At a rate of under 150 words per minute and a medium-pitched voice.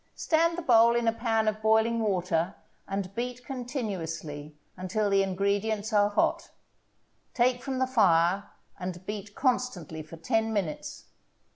No: average, 140 wpm; high, 215 Hz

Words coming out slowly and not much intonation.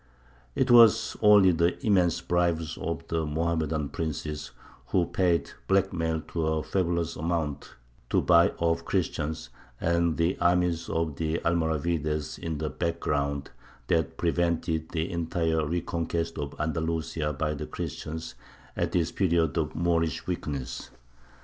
Yes: slow, 130 wpm; narrow, 1.6 semitones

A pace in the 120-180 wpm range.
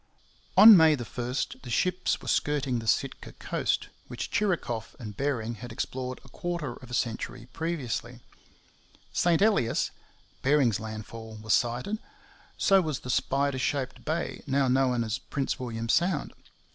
Yes: average, 145 wpm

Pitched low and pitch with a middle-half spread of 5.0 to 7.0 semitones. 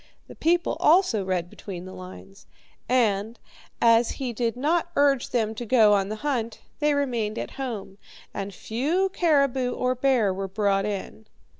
No: high, 230 Hz; average, 5.3 semitones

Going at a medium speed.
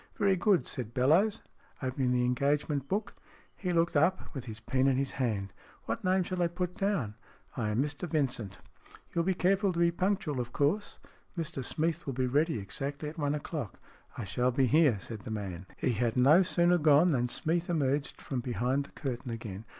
No: fast, 210 wpm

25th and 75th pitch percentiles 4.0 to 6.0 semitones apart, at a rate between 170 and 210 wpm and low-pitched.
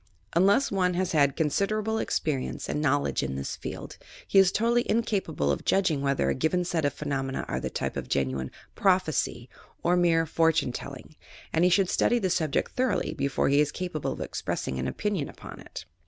No: wide, 5.5 semitones; average, 195 wpm; medium, 160 Hz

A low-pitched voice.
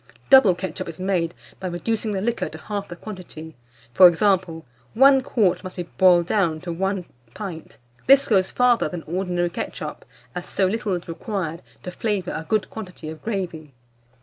No: medium, 185 Hz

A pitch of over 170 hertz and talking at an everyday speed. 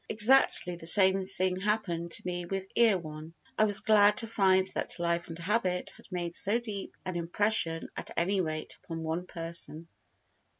Yes: medium, 185 Hz; average, 170 wpm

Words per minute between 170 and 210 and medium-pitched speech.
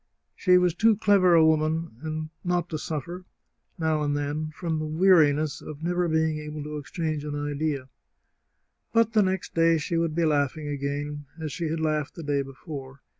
Yes: average, 175 wpm; medium, 155 Hz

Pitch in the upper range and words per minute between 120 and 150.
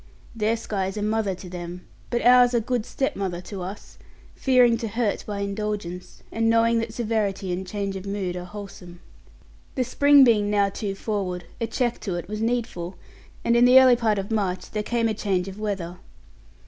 No: high, 210 Hz; average, 195 wpm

